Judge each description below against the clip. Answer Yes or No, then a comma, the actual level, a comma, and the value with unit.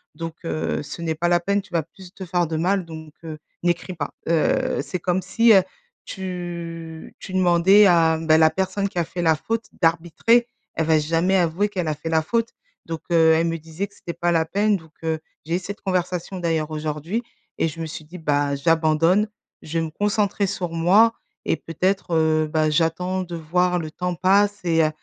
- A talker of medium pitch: Yes, medium, 170 Hz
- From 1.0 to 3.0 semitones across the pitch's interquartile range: Yes, narrow, 2.6 semitones